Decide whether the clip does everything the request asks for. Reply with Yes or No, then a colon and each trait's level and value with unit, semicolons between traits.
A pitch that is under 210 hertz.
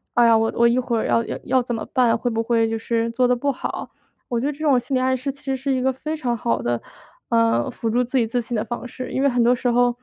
No: high, 245 Hz